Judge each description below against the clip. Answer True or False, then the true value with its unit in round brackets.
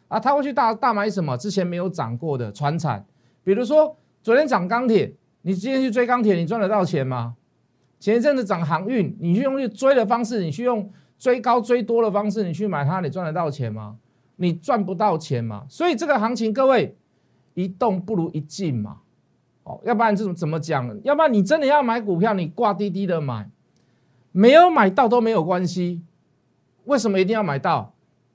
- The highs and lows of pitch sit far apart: True (6.9 semitones)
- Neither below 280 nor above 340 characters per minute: True (290 characters per minute)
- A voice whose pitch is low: False (195 Hz)